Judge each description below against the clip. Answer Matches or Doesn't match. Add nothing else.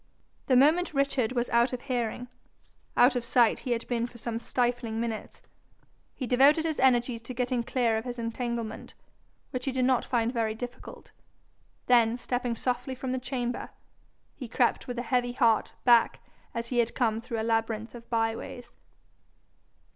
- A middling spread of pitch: Doesn't match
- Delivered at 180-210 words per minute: Doesn't match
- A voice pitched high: Matches